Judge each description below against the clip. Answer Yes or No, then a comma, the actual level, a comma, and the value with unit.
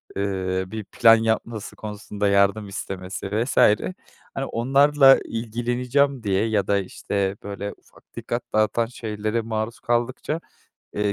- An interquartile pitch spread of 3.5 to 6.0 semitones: No, average, 2.8 semitones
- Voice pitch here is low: Yes, low, 110 Hz